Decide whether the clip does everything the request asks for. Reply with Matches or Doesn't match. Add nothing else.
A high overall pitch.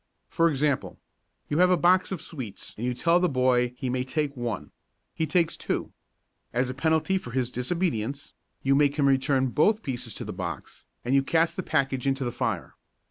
Doesn't match